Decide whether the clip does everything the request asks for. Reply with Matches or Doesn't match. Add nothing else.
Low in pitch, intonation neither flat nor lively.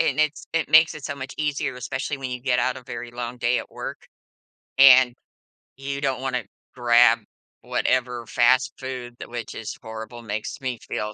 Doesn't match